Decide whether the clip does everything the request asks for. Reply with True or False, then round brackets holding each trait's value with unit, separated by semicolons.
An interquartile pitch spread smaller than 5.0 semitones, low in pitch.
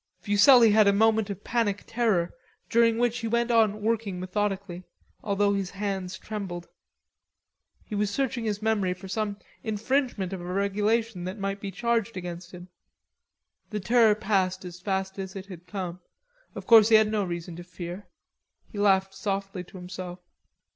False (2.8 semitones; 200 Hz)